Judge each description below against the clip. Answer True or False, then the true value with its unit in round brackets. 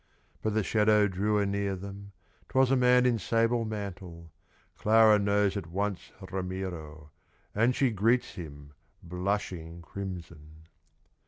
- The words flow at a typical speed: False (120 wpm)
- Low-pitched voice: True (100 Hz)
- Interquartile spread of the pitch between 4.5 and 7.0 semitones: False (3.4 semitones)